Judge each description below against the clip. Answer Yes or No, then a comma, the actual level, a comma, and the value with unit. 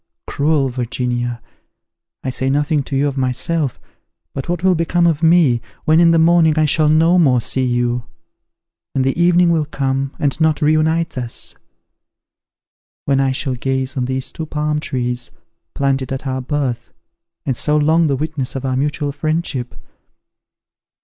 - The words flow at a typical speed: Yes, average, 160 wpm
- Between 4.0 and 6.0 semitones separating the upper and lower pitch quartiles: No, average, 3.3 semitones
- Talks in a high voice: No, medium, 140 Hz